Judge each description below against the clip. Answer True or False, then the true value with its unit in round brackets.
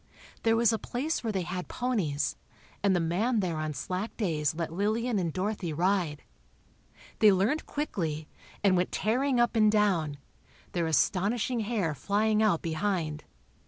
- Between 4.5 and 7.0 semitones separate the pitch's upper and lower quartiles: True (5.0 semitones)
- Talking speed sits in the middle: True (155 wpm)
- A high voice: True (195 Hz)